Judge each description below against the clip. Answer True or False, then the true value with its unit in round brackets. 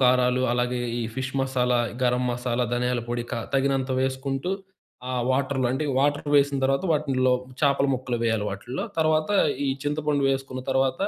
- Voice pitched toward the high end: False (130 Hz)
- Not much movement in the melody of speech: True (1.9 semitones)